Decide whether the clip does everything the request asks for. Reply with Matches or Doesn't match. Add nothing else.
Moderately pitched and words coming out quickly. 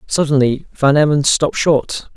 Doesn't match